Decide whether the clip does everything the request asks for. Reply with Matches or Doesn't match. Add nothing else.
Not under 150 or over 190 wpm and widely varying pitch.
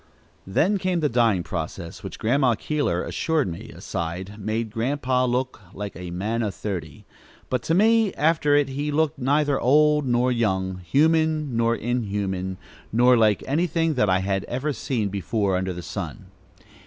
Matches